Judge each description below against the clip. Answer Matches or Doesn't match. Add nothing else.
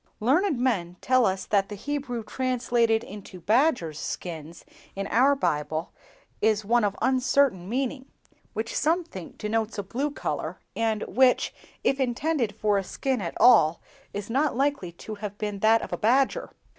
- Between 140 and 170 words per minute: Matches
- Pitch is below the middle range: Doesn't match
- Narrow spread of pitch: Doesn't match